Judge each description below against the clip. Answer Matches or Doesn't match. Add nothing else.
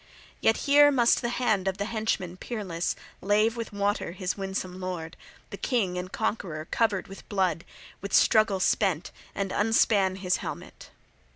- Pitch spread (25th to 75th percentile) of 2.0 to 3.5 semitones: Matches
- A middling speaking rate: Matches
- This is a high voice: Matches